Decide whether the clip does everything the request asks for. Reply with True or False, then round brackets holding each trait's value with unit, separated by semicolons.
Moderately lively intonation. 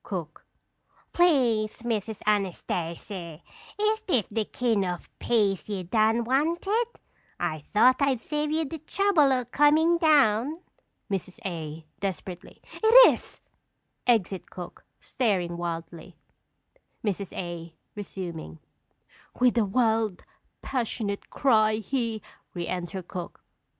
False (6.8 semitones)